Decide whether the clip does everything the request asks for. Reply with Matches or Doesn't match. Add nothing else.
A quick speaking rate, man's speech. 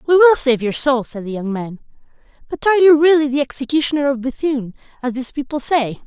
Doesn't match